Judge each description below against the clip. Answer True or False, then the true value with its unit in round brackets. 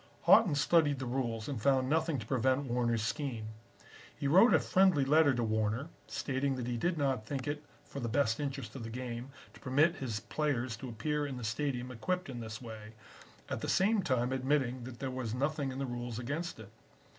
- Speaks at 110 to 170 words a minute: False (205 wpm)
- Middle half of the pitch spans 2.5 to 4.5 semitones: True (3.5 semitones)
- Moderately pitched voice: False (130 Hz)